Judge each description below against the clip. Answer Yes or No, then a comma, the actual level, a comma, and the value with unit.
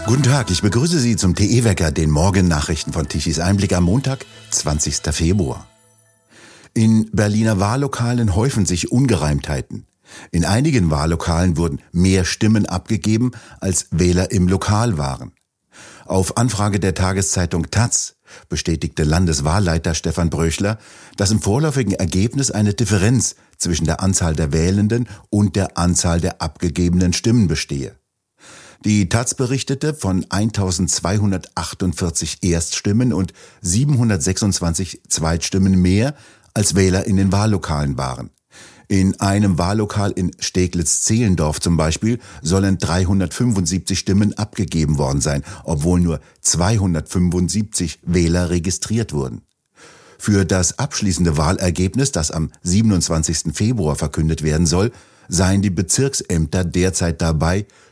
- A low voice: Yes, very low, 95 Hz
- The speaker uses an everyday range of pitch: Yes, average, 4.2 semitones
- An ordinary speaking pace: No, slow, 115 wpm